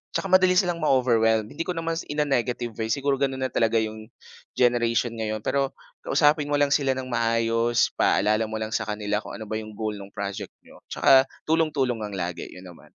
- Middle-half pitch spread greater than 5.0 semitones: No, average, 4.4 semitones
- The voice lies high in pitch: No, low, 115 Hz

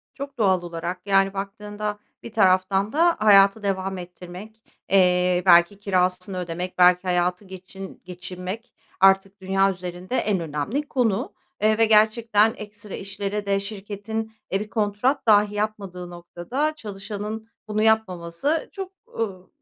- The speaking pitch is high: Yes, high, 195 Hz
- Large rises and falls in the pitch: No, average, 2.9 semitones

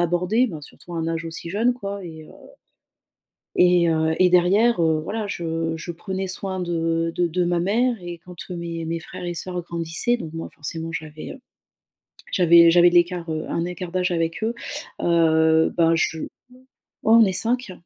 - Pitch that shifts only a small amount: Yes, narrow, 2.1 semitones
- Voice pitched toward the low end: No, medium, 175 Hz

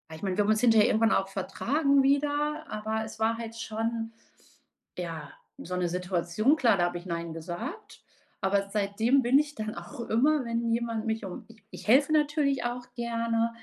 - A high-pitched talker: Yes, high, 225 Hz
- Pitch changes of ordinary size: Yes, average, 3.9 semitones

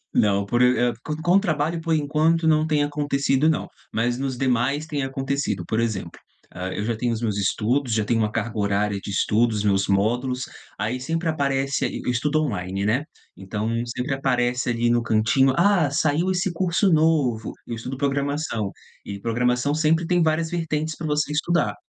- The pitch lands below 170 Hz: Yes, low, 135 Hz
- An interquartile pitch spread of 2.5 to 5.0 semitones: No, wide, 5.5 semitones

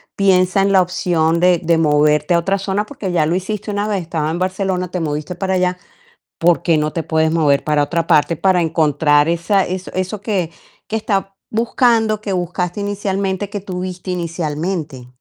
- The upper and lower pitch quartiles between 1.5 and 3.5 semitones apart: Yes, average, 3.2 semitones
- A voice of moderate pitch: Yes, medium, 180 Hz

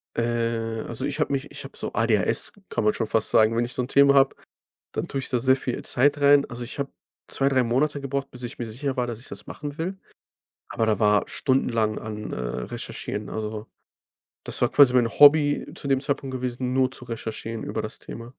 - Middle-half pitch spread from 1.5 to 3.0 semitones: No, average, 3.4 semitones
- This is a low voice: Yes, low, 125 Hz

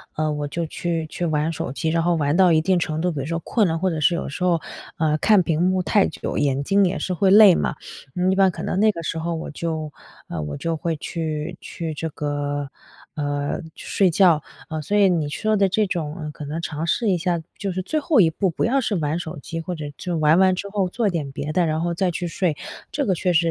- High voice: No, medium, 170 Hz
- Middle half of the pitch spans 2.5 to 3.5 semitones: Yes, average, 3.2 semitones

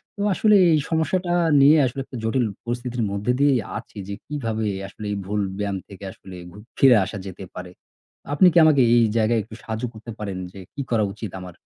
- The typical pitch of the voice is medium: No, low, 115 Hz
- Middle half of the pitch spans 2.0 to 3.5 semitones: No, average, 5.3 semitones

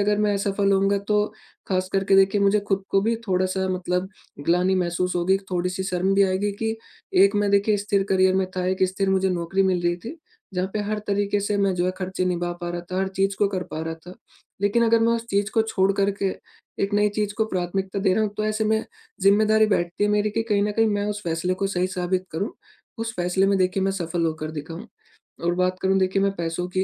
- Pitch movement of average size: No, narrow, 2.0 semitones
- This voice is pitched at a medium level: No, high, 195 Hz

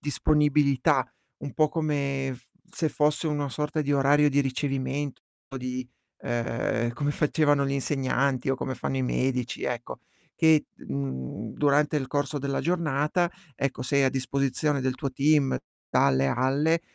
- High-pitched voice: No, medium, 140 Hz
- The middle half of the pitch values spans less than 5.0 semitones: Yes, narrow, 2.4 semitones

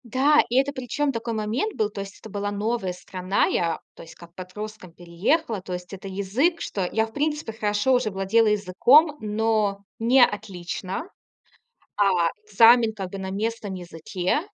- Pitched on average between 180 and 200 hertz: No, high, 210 Hz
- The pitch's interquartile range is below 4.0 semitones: Yes, average, 3.6 semitones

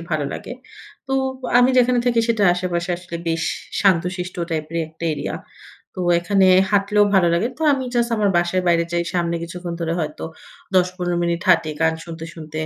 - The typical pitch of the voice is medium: Yes, medium, 175 Hz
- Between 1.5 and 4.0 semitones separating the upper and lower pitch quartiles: Yes, average, 2.9 semitones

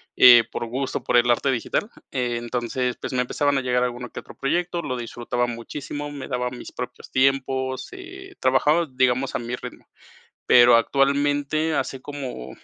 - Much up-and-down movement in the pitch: No, average, 2.8 semitones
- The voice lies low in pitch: Yes, low, 130 Hz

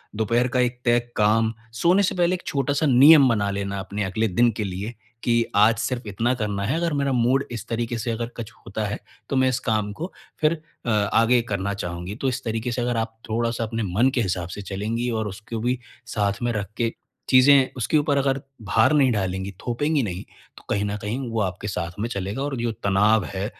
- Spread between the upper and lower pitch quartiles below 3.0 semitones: No, average, 3.7 semitones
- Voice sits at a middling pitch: No, low, 115 Hz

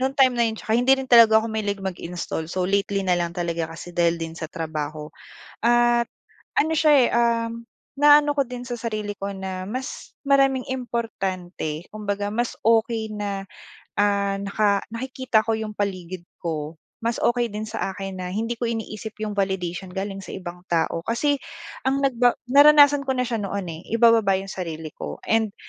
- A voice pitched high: Yes, high, 215 Hz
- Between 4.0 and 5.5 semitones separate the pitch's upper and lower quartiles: Yes, average, 4.3 semitones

